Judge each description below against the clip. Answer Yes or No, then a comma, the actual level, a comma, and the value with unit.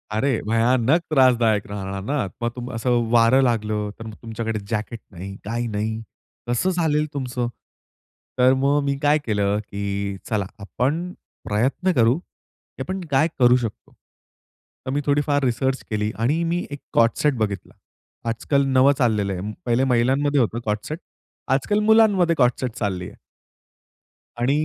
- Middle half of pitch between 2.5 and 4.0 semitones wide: No, average, 4.6 semitones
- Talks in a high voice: No, low, 120 Hz